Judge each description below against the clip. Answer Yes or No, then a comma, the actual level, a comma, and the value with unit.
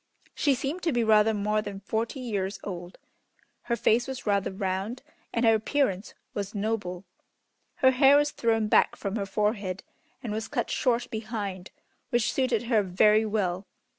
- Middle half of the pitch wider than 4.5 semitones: No, average, 3.3 semitones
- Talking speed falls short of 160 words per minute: No, average, 165 wpm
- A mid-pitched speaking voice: No, high, 215 Hz